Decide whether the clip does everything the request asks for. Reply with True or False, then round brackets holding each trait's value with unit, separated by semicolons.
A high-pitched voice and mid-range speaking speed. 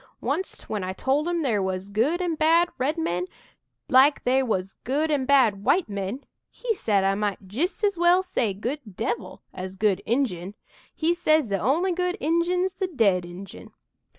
True (260 Hz; 180 wpm)